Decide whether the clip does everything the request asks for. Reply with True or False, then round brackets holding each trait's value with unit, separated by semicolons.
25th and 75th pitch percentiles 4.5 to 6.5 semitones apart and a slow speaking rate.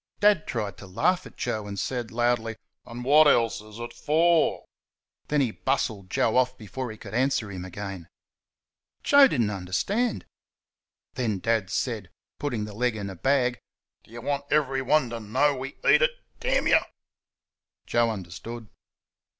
False (4.8 semitones; 160 wpm)